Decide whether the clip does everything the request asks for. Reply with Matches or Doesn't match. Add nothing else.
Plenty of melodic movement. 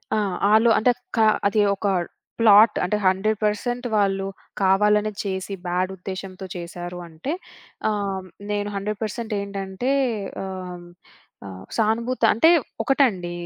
Doesn't match